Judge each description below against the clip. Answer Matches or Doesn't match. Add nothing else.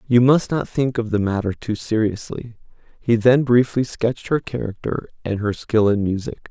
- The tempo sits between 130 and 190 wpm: Matches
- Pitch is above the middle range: Doesn't match